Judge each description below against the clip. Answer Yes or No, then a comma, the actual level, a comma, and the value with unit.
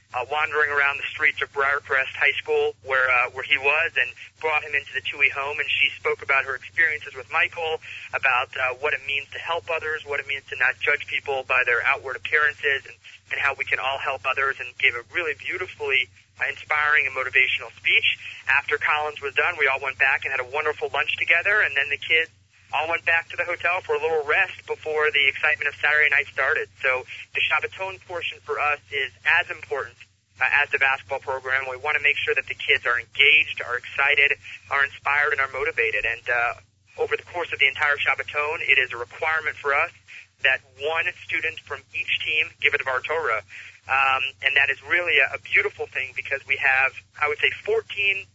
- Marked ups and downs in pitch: No, average, 3.8 semitones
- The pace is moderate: No, fast, 215 wpm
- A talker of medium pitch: Yes, medium, 150 Hz